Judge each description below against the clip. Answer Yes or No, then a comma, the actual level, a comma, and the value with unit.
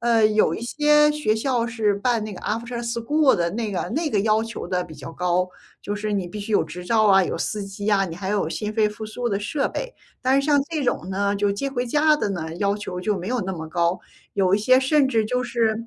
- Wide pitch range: No, average, 3.8 semitones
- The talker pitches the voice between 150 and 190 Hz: No, high, 215 Hz